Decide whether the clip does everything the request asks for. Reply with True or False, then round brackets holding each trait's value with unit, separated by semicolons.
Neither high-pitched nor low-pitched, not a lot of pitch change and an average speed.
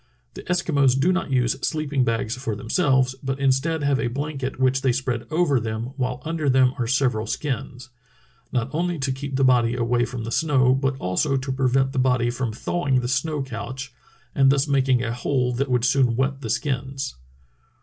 False (130 Hz; 1.9 semitones; 190 wpm)